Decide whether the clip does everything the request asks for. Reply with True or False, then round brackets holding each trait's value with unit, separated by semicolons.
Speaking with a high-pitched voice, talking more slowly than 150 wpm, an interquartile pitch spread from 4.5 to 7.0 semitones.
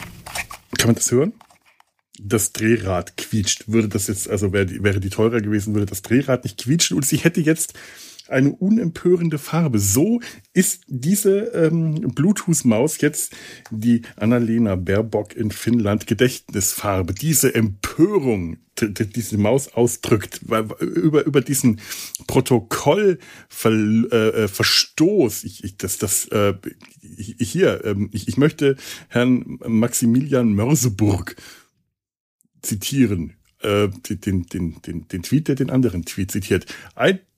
False (115 Hz; 125 wpm; 5.1 semitones)